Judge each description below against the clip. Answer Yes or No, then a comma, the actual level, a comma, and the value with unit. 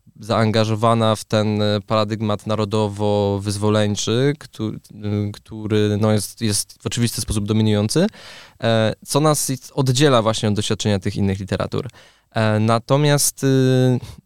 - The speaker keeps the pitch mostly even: Yes, narrow, 2.1 semitones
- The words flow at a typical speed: No, slow, 100 wpm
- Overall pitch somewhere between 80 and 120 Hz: Yes, low, 110 Hz